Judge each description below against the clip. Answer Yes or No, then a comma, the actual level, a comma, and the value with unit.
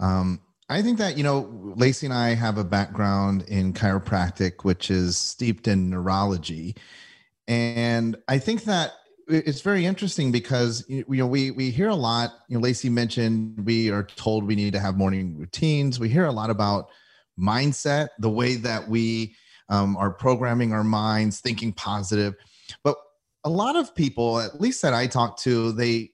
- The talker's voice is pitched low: Yes, low, 115 Hz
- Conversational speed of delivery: Yes, average, 175 wpm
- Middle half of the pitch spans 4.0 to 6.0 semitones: Yes, average, 4.4 semitones